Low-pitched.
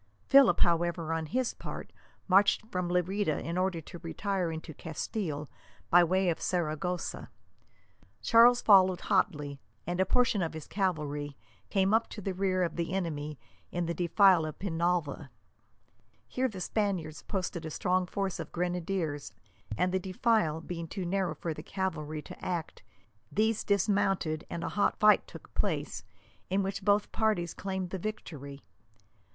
No: medium, 180 Hz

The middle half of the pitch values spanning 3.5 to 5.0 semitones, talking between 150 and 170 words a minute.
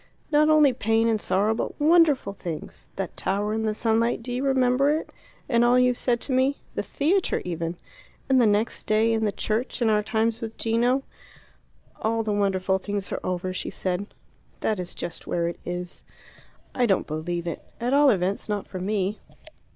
No: average, 4.6 semitones; average, 190 wpm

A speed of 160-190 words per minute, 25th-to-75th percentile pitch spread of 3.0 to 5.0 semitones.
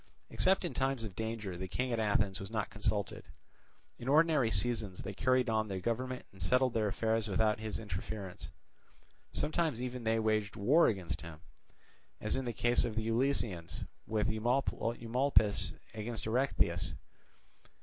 No: average, 150 wpm; average, 3.4 semitones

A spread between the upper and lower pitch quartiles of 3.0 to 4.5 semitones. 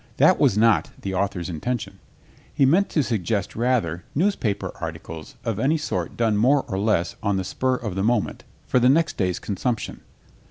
No: average, 5.0 semitones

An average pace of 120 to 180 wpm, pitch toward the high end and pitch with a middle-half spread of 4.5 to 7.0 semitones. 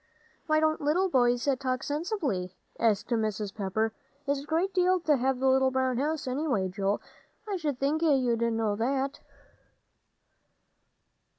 Yes: average, 140 wpm; very high, 265 Hz; average, 5.3 semitones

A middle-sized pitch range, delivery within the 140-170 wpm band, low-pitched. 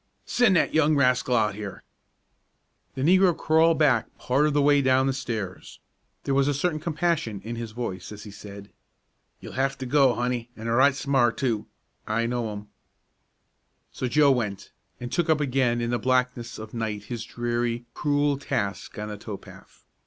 No: average, 4.1 semitones; average, 180 wpm; low, 125 Hz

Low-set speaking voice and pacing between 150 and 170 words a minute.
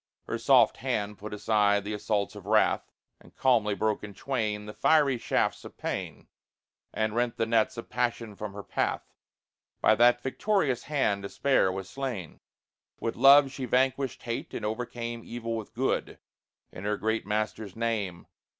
Yes: low, 110 Hz; average, 160 wpm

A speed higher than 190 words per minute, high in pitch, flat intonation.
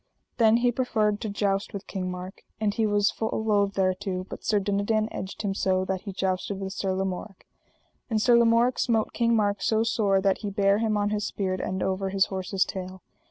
Yes: fast, 205 wpm; high, 200 Hz; narrow, 2.3 semitones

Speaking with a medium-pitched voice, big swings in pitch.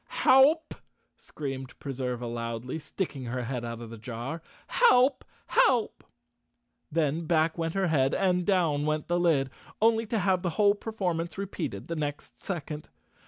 Yes: medium, 160 Hz; wide, 6.5 semitones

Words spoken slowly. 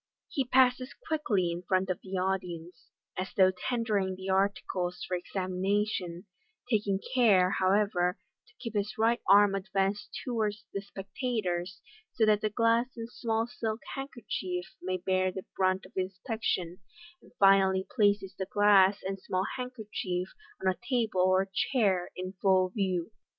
No: average, 150 wpm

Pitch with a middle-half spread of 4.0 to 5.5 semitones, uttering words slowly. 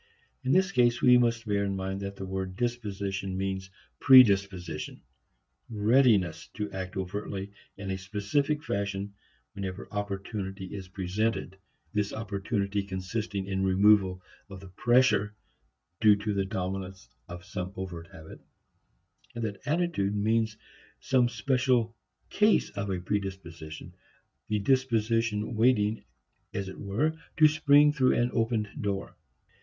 No: average, 3.3 semitones; slow, 130 wpm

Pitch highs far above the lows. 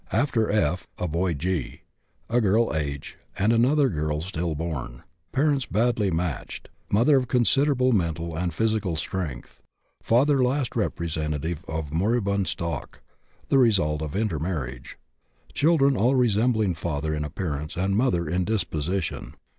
Yes: wide, 6.7 semitones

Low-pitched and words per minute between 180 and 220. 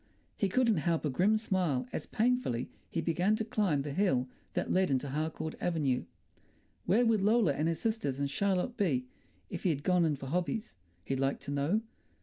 No: medium, 170 Hz; average, 185 wpm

